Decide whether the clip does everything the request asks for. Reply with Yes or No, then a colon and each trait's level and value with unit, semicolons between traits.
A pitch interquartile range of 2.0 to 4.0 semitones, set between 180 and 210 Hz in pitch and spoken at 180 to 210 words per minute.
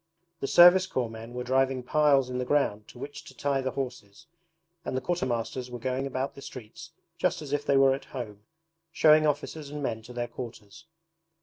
No: average, 2.9 semitones; low, 130 Hz; average, 200 wpm